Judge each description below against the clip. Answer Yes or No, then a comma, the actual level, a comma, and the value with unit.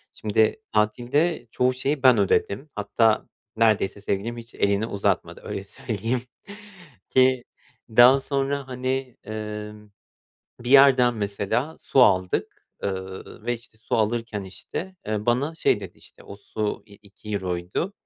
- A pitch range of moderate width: Yes, average, 3.8 semitones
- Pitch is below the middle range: Yes, low, 115 Hz